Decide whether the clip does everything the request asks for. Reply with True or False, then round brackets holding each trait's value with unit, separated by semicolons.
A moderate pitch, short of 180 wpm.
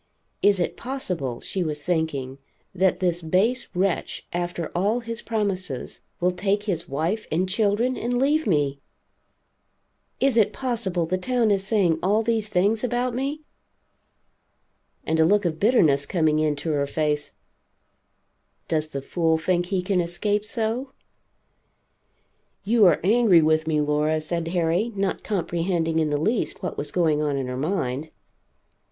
True (180 Hz; 150 wpm)